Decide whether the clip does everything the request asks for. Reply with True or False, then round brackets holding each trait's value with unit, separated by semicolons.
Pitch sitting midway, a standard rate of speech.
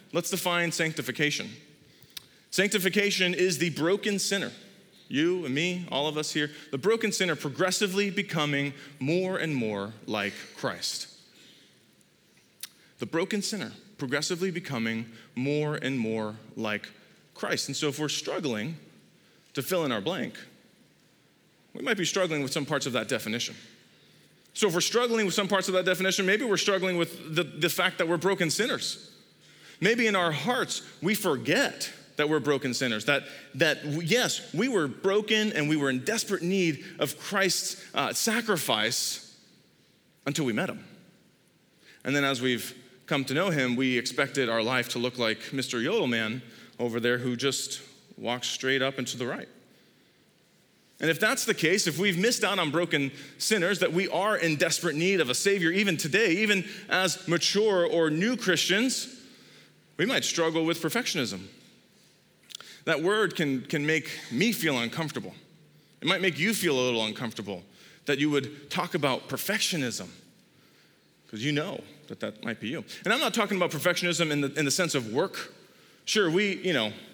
True (165 Hz; 165 wpm)